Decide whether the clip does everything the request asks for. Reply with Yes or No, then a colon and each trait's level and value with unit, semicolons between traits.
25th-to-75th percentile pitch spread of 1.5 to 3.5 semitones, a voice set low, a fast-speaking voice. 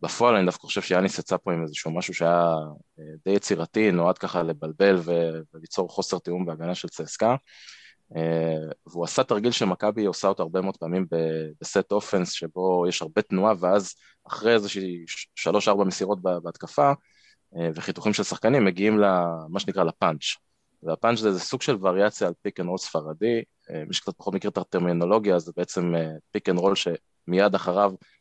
Yes: average, 3.0 semitones; very low, 90 Hz; fast, 155 wpm